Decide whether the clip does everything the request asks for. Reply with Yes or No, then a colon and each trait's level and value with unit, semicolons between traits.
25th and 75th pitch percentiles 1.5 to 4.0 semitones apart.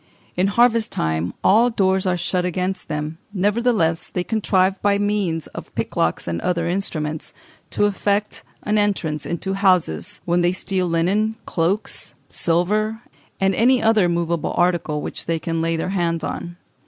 Yes: average, 3.6 semitones